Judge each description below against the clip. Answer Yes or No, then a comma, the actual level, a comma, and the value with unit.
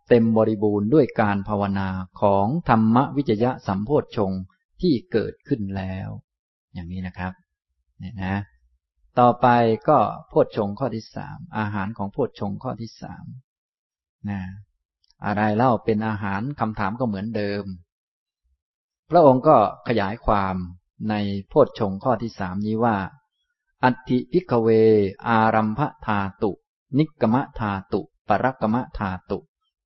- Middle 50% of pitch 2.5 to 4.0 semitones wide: Yes, average, 3.6 semitones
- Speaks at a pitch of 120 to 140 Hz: No, low, 105 Hz